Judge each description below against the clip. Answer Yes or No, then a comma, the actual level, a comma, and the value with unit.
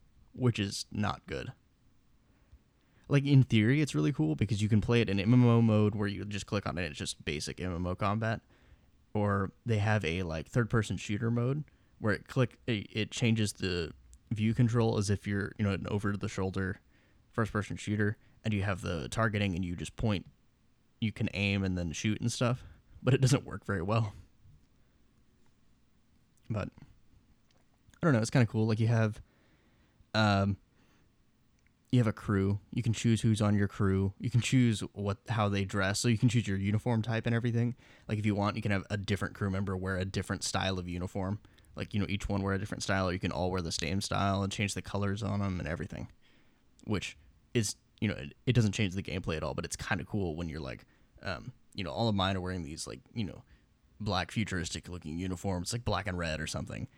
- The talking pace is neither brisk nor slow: No, fast, 210 wpm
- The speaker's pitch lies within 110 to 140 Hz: No, low, 100 Hz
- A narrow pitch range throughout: No, average, 3.1 semitones